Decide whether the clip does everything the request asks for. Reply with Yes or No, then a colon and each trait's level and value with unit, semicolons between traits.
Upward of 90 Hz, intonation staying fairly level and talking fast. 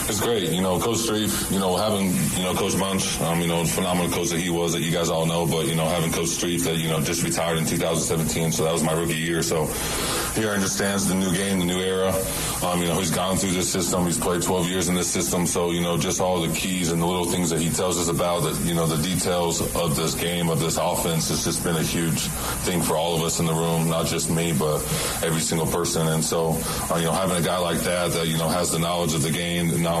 No: very low, 85 Hz; narrow, 1.8 semitones; fast, 265 wpm